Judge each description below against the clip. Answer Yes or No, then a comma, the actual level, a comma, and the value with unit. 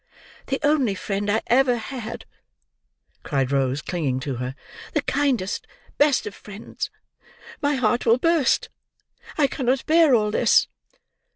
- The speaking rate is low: Yes, slow, 130 wpm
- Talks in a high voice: Yes, high, 235 Hz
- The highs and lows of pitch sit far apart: Yes, wide, 6.7 semitones